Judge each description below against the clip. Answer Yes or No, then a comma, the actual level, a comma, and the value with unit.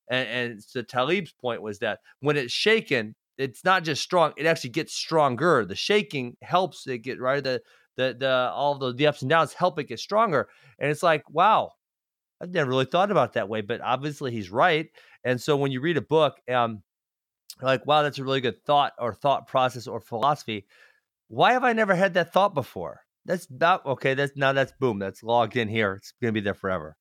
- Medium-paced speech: No, fast, 215 wpm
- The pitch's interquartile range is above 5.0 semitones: No, average, 4.1 semitones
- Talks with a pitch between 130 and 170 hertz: Yes, low, 135 Hz